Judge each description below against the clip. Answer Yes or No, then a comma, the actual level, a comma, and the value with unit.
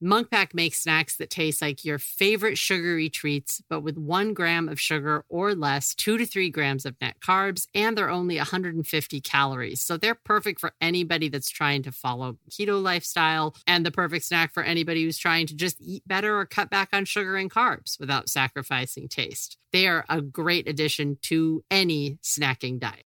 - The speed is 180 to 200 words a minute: Yes, average, 185 wpm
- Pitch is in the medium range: Yes, medium, 165 Hz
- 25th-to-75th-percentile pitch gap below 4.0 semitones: No, average, 4.3 semitones